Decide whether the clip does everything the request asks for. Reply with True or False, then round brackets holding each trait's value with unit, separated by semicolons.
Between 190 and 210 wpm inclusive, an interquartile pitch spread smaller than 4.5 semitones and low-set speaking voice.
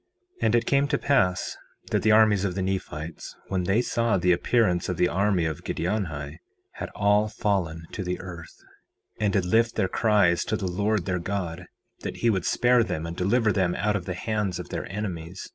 True (205 wpm; 3.4 semitones; 95 Hz)